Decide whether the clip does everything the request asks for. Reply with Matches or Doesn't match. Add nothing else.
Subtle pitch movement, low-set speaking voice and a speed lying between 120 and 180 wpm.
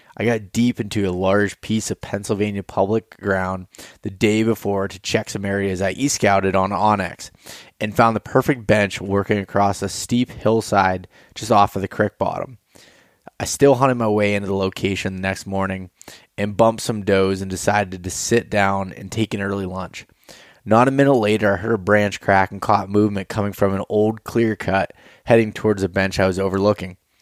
Doesn't match